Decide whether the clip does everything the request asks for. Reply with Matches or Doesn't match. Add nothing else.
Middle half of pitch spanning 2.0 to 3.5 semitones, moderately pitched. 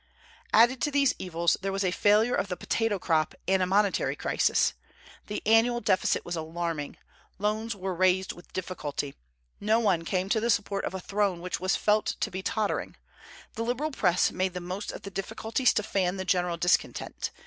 Doesn't match